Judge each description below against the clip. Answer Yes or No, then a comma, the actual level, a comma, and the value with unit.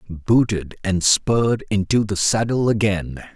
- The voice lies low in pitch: Yes, low, 105 Hz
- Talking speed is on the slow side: Yes, slow, 125 wpm